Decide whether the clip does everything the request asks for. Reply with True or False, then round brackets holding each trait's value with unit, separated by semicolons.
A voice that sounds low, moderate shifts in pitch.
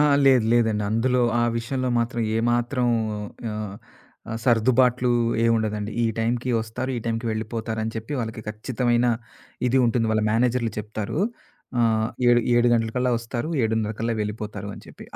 False (115 Hz; 1.8 semitones)